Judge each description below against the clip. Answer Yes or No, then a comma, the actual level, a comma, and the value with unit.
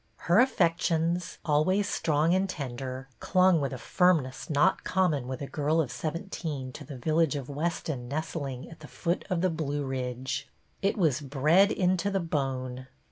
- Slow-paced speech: No, average, 170 wpm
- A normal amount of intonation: Yes, average, 4.5 semitones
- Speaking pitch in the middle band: Yes, medium, 155 Hz